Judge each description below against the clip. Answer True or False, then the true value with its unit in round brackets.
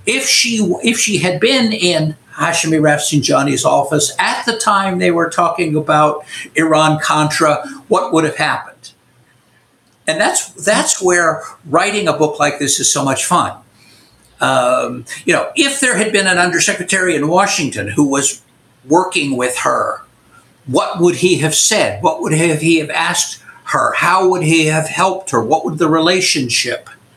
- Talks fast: False (160 wpm)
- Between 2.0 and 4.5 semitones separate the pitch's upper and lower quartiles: True (3.5 semitones)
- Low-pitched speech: False (165 Hz)